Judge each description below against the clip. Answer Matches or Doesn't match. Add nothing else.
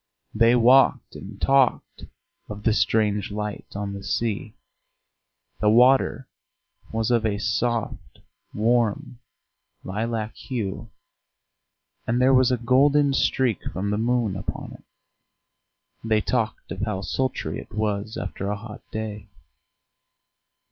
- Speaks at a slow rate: Matches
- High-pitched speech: Doesn't match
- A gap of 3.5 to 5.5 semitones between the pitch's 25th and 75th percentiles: Doesn't match